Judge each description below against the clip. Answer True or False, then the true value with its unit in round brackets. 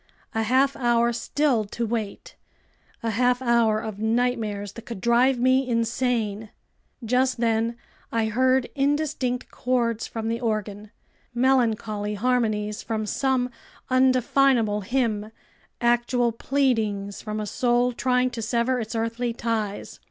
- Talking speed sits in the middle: False (125 wpm)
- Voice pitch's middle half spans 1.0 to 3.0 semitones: True (2.5 semitones)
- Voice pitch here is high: True (235 Hz)